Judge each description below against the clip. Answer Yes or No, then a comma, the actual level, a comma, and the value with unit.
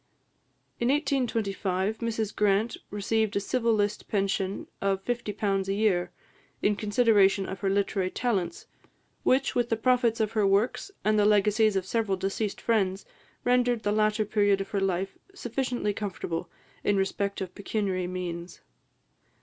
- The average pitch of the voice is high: Yes, high, 205 Hz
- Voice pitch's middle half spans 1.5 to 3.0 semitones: Yes, narrow, 2.6 semitones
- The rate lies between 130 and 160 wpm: Yes, average, 145 wpm